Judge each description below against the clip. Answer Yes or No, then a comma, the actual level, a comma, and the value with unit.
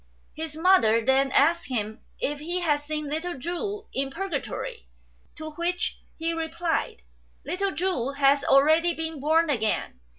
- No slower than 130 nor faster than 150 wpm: Yes, average, 145 wpm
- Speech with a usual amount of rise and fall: Yes, average, 3.8 semitones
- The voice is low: No, very high, 315 Hz